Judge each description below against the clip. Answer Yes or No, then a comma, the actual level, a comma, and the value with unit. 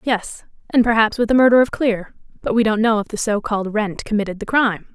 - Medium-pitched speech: No, high, 220 Hz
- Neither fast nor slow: No, fast, 230 wpm